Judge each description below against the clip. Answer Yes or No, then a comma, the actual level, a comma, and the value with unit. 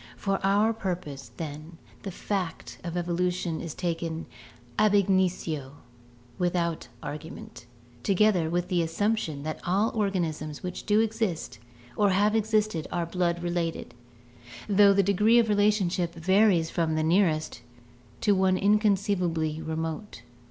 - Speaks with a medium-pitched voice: Yes, medium, 180 Hz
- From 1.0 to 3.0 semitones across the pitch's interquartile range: No, average, 3.8 semitones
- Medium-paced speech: No, slow, 125 wpm